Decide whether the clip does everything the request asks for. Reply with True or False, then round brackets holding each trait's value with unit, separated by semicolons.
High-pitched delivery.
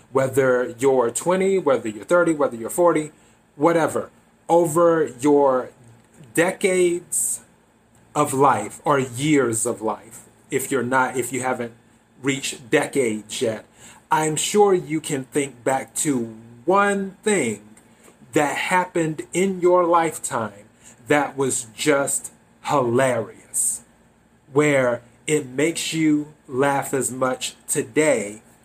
False (140 Hz)